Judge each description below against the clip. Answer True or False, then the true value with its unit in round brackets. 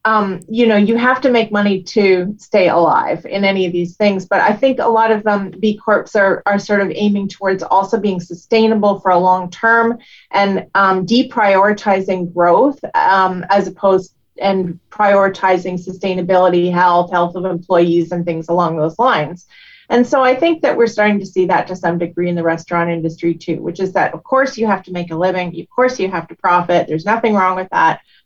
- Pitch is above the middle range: True (195 Hz)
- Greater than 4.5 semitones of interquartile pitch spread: False (3.2 semitones)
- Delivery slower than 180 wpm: False (205 wpm)